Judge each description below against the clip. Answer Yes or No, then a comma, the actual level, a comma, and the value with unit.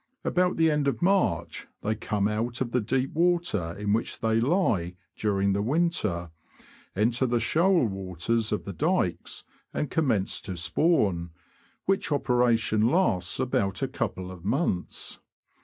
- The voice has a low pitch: Yes, low, 115 Hz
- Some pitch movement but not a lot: No, wide, 7.4 semitones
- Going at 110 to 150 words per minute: Yes, average, 145 wpm